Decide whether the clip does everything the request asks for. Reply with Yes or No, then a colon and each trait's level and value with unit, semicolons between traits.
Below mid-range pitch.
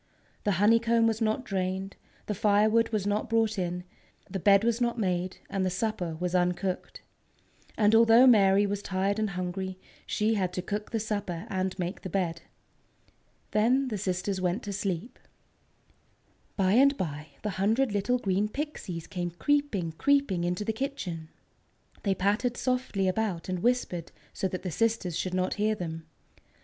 No: high, 200 Hz